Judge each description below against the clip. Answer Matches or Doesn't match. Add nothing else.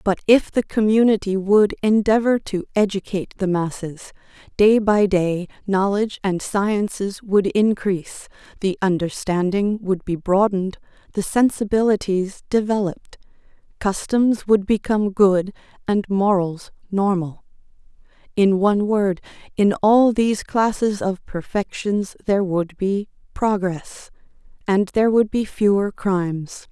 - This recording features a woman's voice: Matches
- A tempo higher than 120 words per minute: Doesn't match